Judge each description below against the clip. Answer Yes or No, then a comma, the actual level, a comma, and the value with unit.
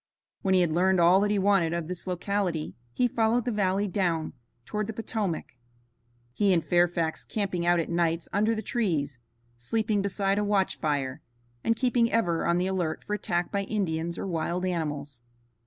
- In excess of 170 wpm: Yes, average, 180 wpm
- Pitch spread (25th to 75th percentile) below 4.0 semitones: Yes, average, 3.6 semitones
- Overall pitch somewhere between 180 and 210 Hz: Yes, medium, 185 Hz